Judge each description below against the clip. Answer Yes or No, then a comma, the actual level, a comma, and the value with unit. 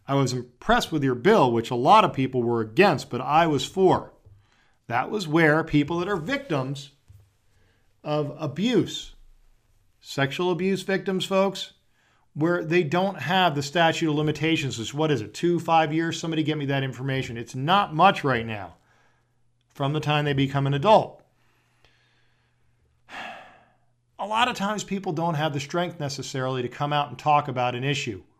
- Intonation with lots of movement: Yes, wide, 5.7 semitones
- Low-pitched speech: No, medium, 145 Hz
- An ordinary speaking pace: Yes, average, 170 wpm